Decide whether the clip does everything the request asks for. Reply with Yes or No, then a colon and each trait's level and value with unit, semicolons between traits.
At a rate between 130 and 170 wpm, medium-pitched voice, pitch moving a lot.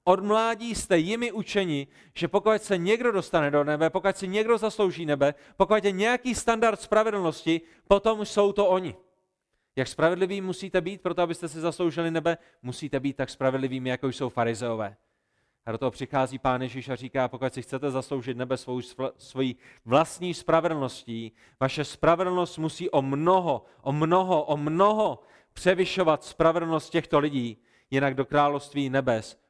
Yes: average, 155 wpm; medium, 160 Hz; wide, 6.1 semitones